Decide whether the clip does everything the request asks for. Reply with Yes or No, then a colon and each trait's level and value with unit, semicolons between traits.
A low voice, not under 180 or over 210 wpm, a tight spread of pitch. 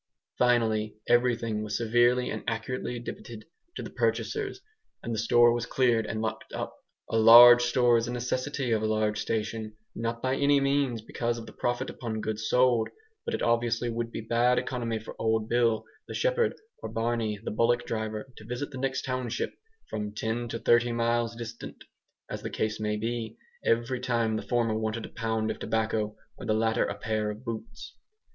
Yes: low, 115 Hz; average, 185 wpm; narrow, 1.7 semitones